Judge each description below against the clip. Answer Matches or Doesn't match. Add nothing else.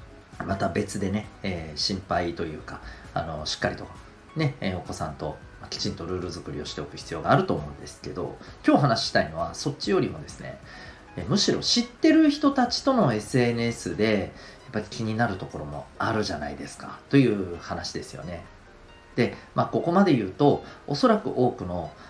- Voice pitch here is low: Matches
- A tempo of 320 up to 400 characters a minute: Matches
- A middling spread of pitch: Doesn't match